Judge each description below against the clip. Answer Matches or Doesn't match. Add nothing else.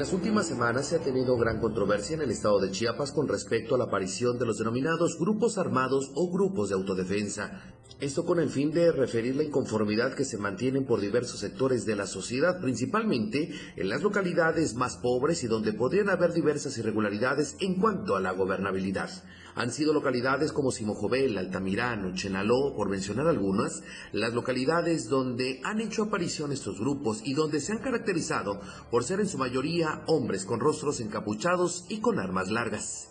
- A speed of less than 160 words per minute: Doesn't match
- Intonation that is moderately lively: Doesn't match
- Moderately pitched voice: Doesn't match